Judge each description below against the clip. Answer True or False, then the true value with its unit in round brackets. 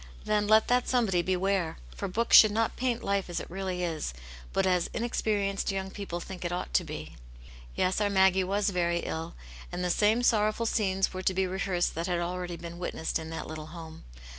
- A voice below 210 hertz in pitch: True (190 Hz)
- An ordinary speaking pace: False (210 wpm)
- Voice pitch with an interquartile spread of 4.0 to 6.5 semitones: False (3.0 semitones)